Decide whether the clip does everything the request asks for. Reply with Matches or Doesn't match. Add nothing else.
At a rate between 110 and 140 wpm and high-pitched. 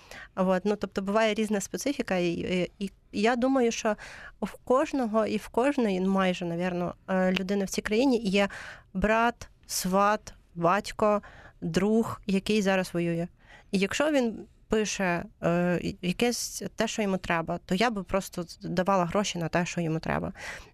Doesn't match